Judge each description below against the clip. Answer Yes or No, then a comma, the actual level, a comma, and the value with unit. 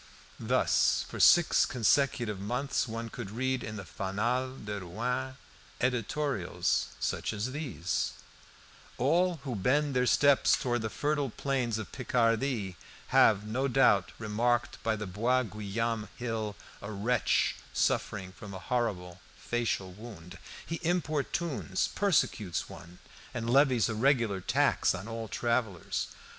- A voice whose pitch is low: Yes, low, 115 Hz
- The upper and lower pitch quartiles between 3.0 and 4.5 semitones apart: Yes, average, 4.1 semitones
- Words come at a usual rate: No, slow, 130 wpm